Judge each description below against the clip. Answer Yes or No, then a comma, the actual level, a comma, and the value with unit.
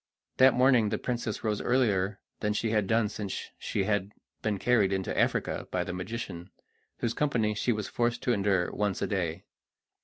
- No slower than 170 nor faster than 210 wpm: Yes, average, 180 wpm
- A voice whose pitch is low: Yes, low, 105 Hz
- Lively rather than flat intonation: No, average, 3.3 semitones